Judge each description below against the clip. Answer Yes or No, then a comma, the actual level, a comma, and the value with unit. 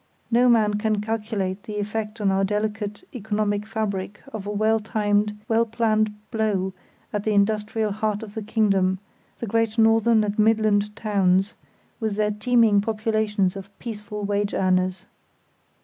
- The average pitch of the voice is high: Yes, high, 210 Hz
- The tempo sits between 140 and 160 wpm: Yes, average, 150 wpm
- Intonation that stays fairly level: Yes, narrow, 1.4 semitones